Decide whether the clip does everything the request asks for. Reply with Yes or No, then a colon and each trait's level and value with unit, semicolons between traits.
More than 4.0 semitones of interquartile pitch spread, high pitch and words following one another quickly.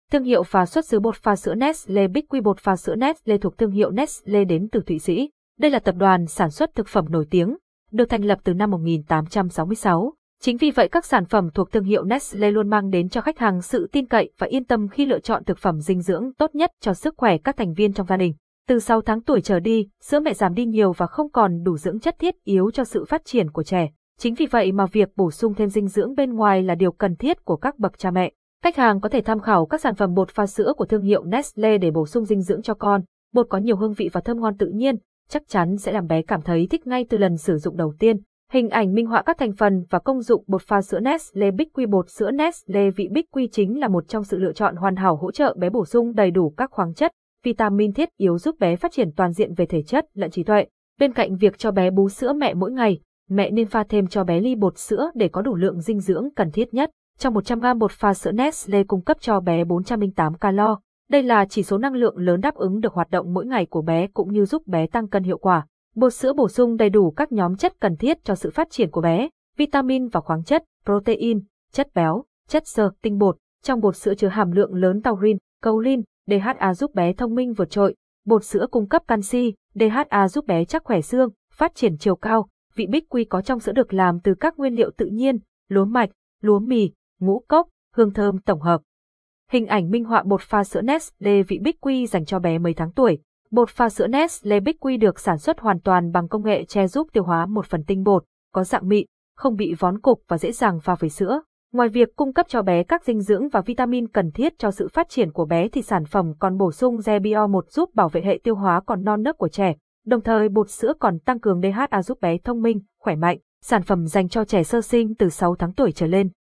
Yes: average, 4.6 semitones; high, 210 Hz; fast, 255 wpm